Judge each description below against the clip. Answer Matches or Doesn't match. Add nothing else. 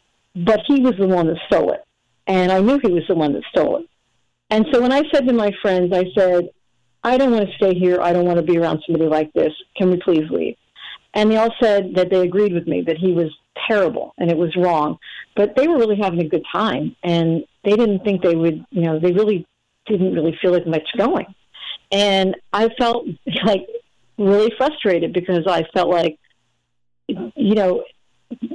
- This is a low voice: Doesn't match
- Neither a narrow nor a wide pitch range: Matches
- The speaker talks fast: Matches